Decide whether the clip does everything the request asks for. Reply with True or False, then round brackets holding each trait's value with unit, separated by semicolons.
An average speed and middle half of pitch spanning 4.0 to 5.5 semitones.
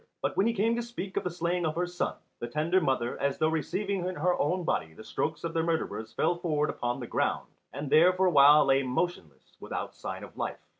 False (240 wpm; 4.3 semitones)